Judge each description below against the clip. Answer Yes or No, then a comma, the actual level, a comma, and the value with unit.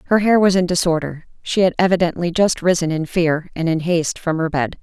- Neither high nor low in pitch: Yes, medium, 170 Hz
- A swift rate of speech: Yes, fast, 225 wpm